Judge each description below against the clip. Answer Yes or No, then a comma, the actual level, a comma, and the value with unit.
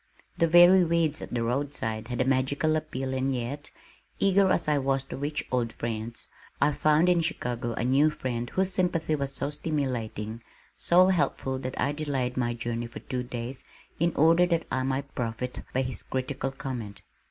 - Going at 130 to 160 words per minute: No, average, 180 wpm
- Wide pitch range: No, average, 4.1 semitones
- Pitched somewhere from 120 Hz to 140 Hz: Yes, low, 135 Hz